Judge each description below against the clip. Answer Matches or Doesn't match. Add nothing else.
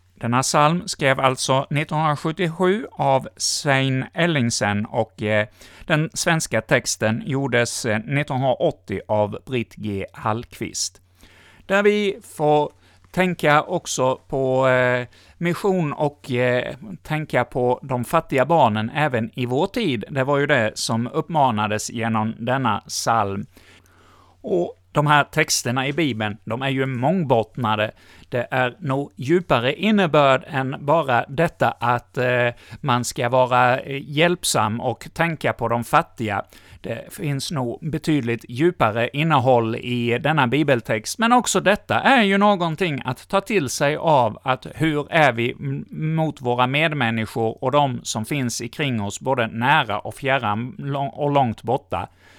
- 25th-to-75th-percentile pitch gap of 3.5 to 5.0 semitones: Matches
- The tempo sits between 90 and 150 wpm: Matches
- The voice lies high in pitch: Doesn't match